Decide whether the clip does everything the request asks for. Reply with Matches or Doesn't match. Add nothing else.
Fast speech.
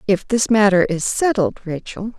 Doesn't match